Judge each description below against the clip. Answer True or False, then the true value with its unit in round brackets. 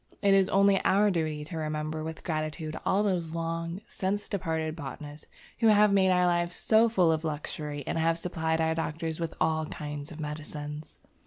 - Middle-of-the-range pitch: True (160 Hz)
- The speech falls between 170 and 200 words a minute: True (180 wpm)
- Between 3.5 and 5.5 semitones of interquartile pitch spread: False (3.1 semitones)